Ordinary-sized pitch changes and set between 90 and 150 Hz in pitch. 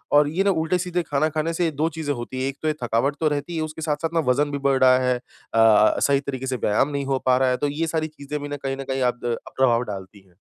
Yes: average, 3.5 semitones; medium, 140 Hz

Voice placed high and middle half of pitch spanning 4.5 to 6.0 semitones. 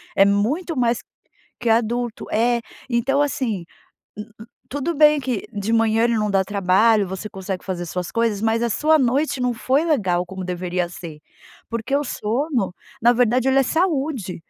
Yes: high, 230 Hz; average, 5.0 semitones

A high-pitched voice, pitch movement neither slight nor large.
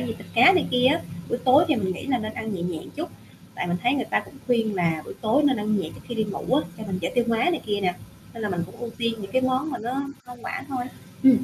Yes: high, 230 Hz; average, 4.2 semitones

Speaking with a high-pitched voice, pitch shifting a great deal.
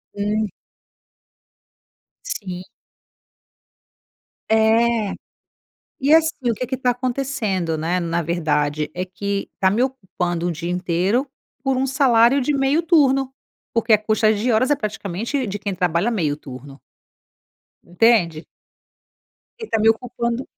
Yes: high, 220 Hz; wide, 6.1 semitones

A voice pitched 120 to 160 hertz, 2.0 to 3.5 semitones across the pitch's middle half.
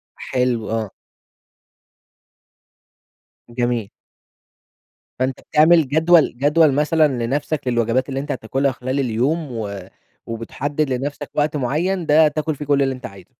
No: low, 135 Hz; average, 3.9 semitones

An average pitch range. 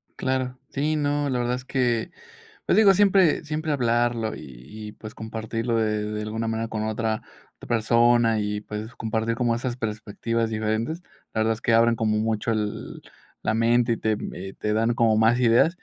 No: narrow, 1.9 semitones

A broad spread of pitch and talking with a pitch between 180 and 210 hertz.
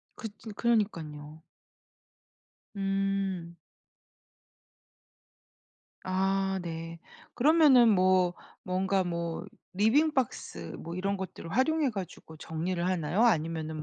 No: average, 4.0 semitones; medium, 185 Hz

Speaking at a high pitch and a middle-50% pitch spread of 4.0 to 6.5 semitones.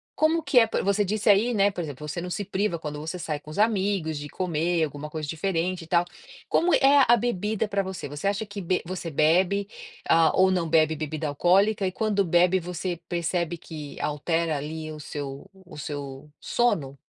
No: medium, 175 Hz; average, 4.4 semitones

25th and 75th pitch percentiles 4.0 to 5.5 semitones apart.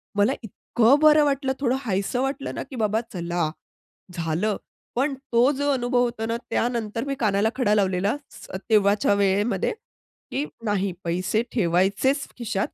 Yes: average, 4.9 semitones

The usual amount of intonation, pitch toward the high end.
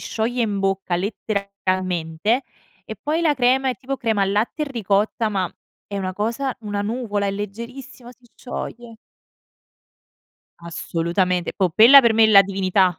Yes: average, 3.9 semitones; high, 210 Hz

